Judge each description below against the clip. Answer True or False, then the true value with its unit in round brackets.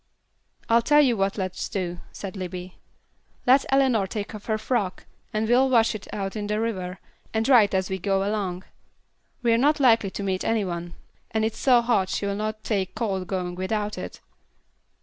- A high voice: True (210 Hz)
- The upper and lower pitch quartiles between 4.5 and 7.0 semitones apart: False (3.3 semitones)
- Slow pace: False (190 wpm)